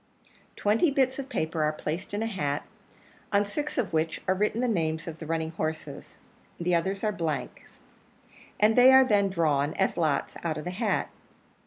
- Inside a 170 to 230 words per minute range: Yes, average, 185 wpm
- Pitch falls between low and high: Yes, medium, 180 Hz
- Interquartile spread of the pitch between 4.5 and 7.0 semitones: Yes, average, 5.2 semitones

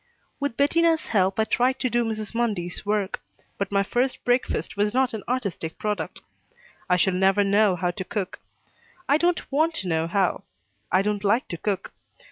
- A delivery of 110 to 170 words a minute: No, average, 180 wpm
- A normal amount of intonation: Yes, average, 4.5 semitones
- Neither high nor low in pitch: No, high, 210 Hz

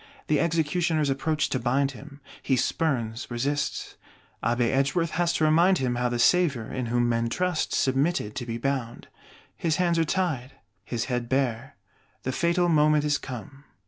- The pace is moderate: Yes, average, 165 wpm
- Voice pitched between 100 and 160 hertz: Yes, medium, 140 Hz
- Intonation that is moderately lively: Yes, average, 4.7 semitones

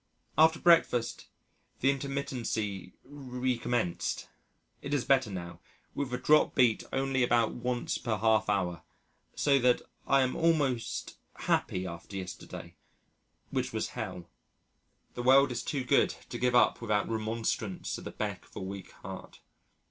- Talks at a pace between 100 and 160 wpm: Yes, average, 140 wpm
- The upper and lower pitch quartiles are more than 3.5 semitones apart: Yes, average, 4.2 semitones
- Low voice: Yes, low, 120 Hz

